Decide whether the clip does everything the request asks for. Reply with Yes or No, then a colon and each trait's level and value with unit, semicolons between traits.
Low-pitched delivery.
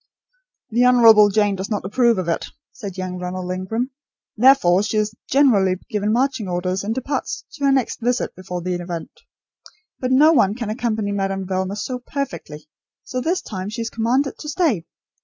No: high, 215 Hz